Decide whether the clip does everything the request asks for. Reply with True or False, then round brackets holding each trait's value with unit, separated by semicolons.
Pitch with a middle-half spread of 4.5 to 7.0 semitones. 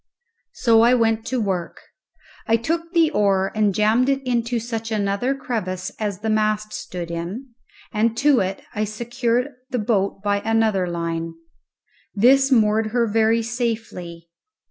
False (3.1 semitones)